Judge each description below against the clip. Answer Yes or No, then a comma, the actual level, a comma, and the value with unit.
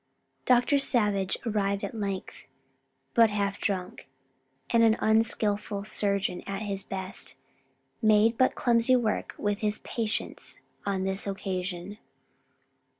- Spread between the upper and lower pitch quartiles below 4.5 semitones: Yes, narrow, 2.4 semitones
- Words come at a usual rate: No, slow, 115 wpm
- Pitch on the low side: No, high, 205 Hz